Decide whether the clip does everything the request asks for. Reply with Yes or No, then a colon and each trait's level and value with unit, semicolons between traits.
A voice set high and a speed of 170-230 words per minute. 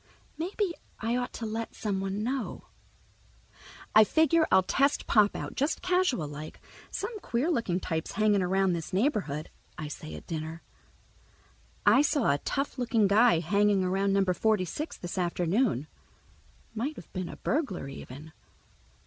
No: high, 205 Hz; average, 150 wpm